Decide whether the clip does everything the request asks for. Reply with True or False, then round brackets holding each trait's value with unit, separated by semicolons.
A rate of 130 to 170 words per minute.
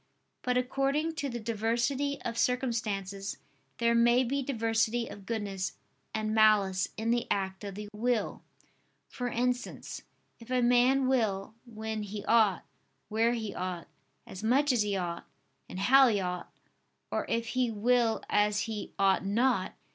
True (150 wpm)